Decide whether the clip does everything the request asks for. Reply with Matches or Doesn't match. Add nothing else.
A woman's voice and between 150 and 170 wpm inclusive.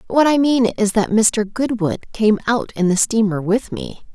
Doesn't match